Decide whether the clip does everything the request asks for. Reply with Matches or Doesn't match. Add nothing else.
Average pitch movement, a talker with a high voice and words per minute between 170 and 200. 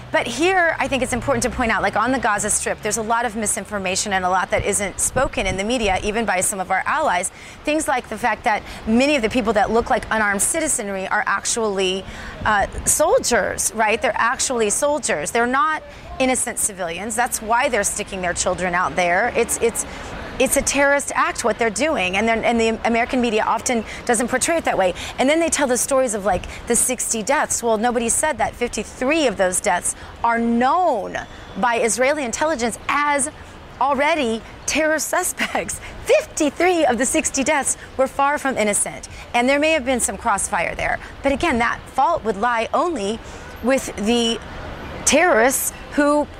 Matches